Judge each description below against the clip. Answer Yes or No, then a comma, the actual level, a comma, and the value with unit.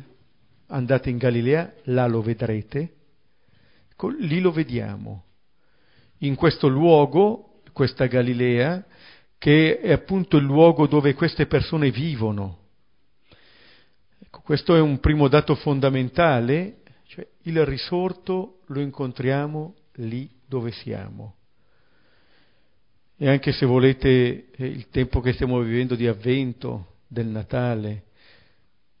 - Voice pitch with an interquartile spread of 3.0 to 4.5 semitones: Yes, average, 4.2 semitones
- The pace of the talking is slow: Yes, slow, 110 wpm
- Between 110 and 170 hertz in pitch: Yes, low, 135 Hz